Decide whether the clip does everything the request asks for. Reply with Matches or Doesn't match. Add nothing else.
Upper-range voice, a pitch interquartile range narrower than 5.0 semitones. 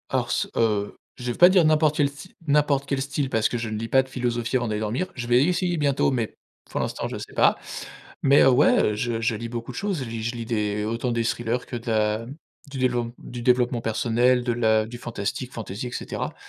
Doesn't match